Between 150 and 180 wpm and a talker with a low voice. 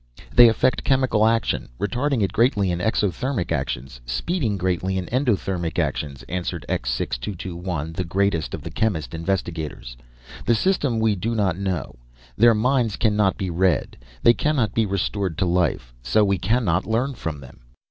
Yes: average, 155 wpm; very low, 95 Hz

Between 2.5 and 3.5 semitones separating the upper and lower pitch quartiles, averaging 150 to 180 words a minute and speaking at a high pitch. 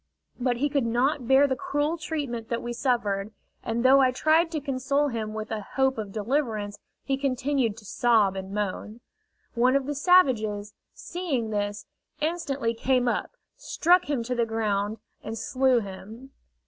No: average, 4.3 semitones; average, 165 wpm; high, 245 Hz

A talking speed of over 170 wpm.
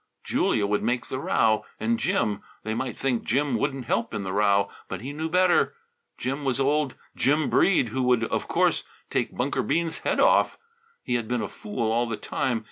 Yes: average, 200 wpm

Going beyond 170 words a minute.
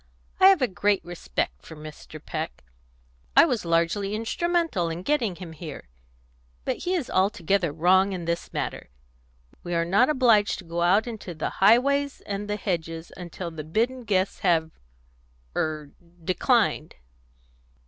No: average, 150 wpm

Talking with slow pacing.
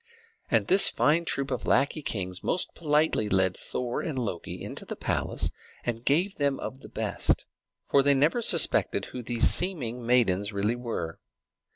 No: average, 165 wpm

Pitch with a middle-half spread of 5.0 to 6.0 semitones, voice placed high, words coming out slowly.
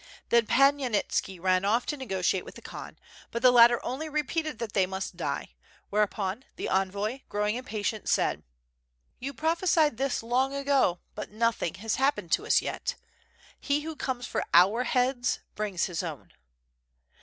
No: wide, 5.4 semitones; high, 235 Hz; average, 165 wpm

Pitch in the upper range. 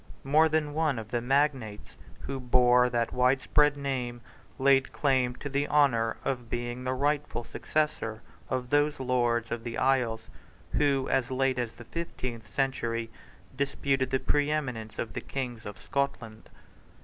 No: low, 130 Hz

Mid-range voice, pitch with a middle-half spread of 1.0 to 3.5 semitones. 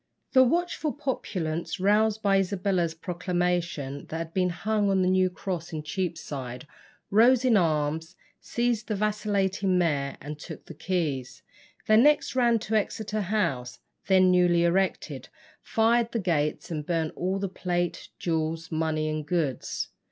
No: medium, 180 Hz; average, 4.6 semitones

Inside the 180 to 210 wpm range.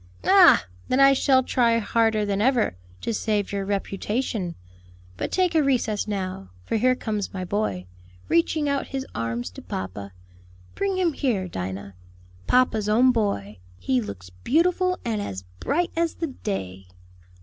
No: average, 150 wpm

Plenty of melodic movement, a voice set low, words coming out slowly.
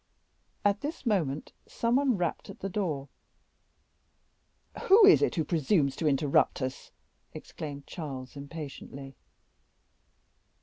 No: wide, 6.6 semitones; medium, 155 Hz; slow, 115 wpm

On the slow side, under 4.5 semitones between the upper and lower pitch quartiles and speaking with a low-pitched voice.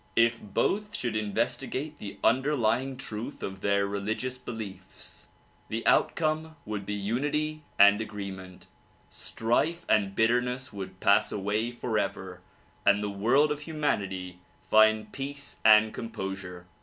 No: slow, 125 wpm; average, 4.8 semitones; low, 110 Hz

